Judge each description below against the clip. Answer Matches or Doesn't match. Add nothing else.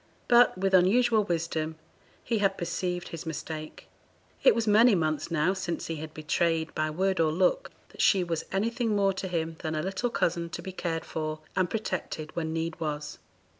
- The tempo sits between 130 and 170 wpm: Doesn't match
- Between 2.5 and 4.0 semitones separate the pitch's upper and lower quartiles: Matches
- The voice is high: Doesn't match